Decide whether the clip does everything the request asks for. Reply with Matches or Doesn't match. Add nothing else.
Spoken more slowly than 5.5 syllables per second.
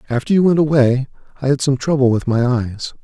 Doesn't match